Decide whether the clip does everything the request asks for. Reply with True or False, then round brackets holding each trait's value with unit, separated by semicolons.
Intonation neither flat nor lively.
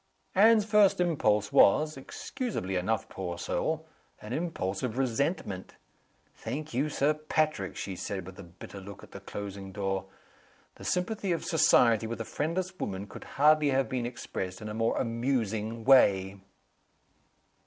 False (7.7 semitones)